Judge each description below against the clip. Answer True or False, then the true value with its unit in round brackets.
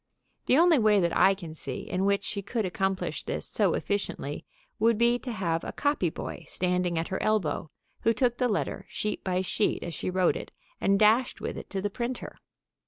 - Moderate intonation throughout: True (4.0 semitones)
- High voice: True (200 Hz)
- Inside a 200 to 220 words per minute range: True (205 wpm)